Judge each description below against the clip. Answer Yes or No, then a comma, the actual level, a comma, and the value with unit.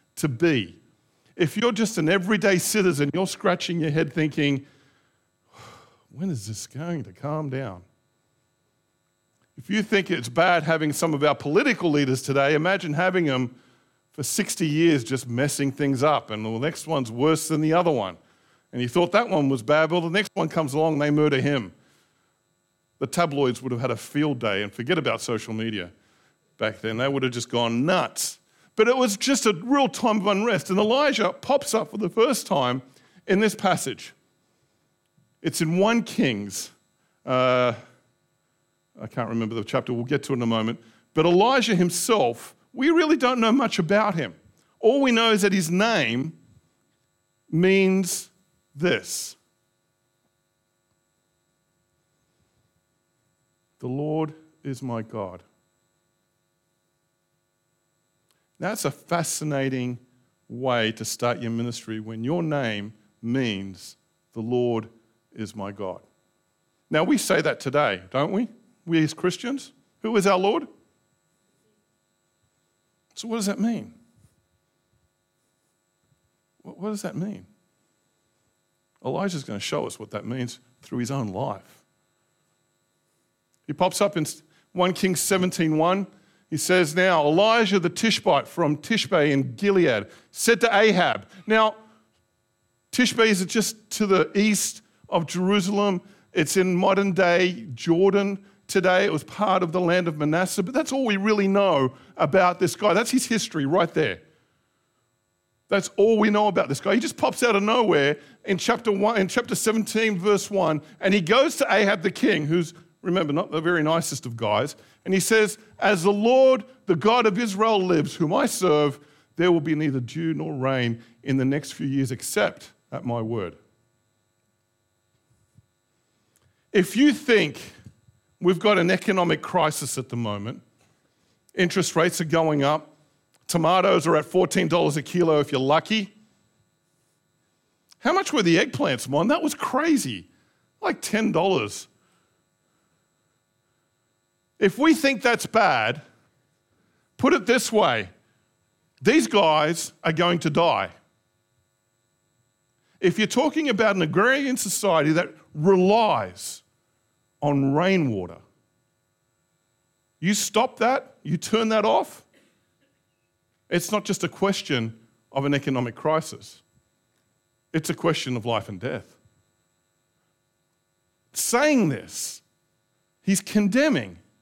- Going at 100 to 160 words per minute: Yes, average, 145 wpm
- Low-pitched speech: No, medium, 170 Hz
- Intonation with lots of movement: Yes, wide, 7.4 semitones